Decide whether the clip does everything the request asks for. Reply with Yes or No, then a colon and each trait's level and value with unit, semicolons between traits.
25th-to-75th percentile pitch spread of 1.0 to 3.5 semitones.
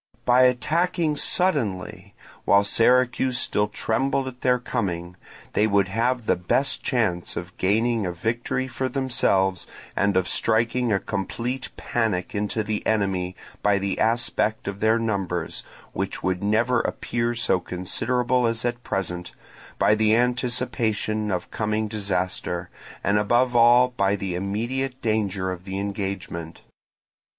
No: average, 3.9 semitones